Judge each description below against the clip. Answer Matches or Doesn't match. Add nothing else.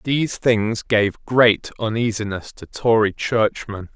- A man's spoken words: Matches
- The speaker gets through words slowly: Matches